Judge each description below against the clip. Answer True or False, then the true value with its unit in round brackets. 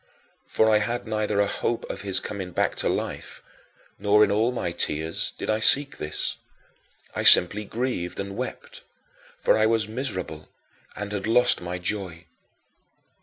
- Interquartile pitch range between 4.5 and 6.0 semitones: False (3.4 semitones)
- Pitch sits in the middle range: False (105 Hz)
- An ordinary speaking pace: True (160 wpm)